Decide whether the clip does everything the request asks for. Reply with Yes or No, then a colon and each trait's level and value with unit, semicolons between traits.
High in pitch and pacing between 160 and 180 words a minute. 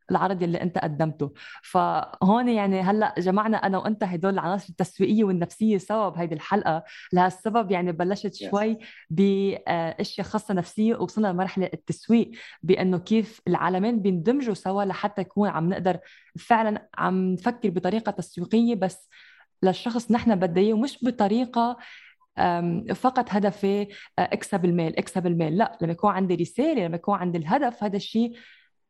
No: high, 195 Hz; slow, 135 wpm